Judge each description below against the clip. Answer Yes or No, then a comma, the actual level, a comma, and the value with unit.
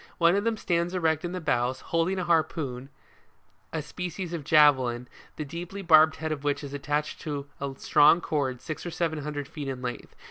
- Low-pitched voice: No, medium, 155 Hz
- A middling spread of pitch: Yes, average, 3.3 semitones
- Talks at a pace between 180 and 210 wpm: Yes, average, 200 wpm